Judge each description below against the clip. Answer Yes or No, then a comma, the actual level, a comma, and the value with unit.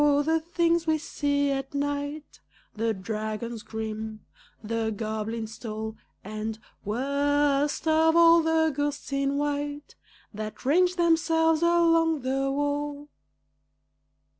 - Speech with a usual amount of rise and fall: No, wide, 6.0 semitones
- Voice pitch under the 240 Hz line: No, very high, 285 Hz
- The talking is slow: Yes, slow, 110 wpm